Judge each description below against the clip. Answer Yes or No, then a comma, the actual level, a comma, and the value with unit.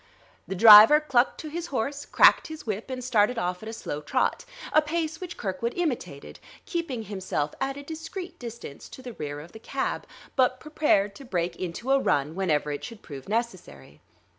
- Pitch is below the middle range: No, high, 235 Hz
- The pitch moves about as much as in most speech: No, wide, 7.3 semitones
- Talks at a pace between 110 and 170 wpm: No, average, 190 wpm